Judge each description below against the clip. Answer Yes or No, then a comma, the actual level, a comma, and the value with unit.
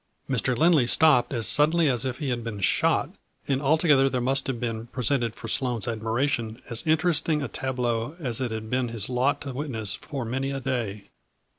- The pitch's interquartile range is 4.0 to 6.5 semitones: No, average, 3.3 semitones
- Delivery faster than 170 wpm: Yes, average, 190 wpm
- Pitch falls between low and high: No, low, 125 Hz